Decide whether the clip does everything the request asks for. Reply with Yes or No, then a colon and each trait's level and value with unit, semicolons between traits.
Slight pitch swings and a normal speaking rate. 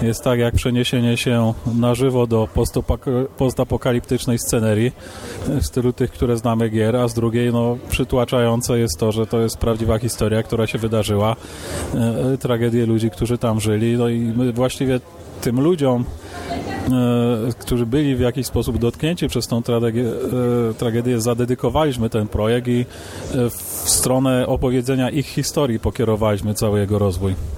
Yes: narrow, 2.0 semitones; average, 150 wpm